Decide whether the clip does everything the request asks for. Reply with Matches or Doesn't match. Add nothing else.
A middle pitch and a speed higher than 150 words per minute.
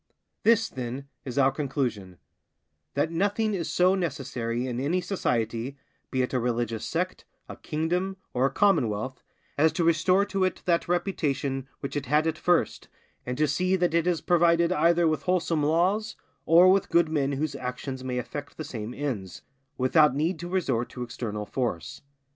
Matches